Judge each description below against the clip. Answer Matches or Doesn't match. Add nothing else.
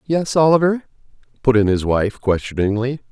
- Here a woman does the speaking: Doesn't match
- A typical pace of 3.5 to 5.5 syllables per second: Matches